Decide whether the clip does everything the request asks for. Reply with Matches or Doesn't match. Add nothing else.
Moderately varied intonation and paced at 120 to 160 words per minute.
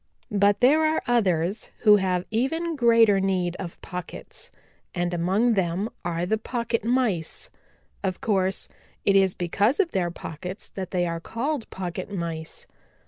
Matches